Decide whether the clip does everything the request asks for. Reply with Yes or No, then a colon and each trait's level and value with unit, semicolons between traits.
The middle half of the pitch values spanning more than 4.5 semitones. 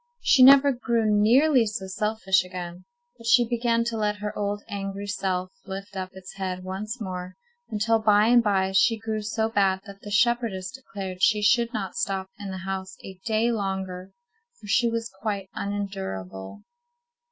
No: average, 3.0 semitones